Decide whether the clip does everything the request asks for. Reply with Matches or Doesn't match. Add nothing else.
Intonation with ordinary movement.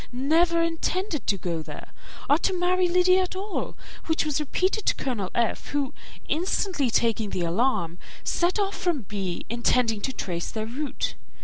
Doesn't match